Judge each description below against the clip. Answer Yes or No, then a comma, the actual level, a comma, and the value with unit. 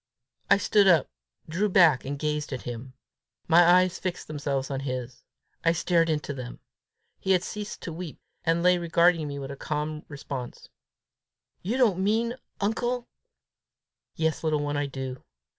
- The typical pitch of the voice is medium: Yes, medium, 160 Hz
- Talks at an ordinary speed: Yes, average, 160 wpm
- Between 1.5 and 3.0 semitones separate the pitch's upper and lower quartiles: No, average, 4.4 semitones